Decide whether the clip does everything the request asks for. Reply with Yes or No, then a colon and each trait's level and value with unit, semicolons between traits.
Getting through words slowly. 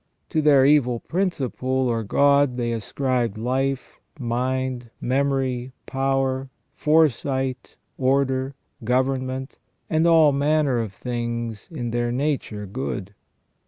Yes: slow, 105 wpm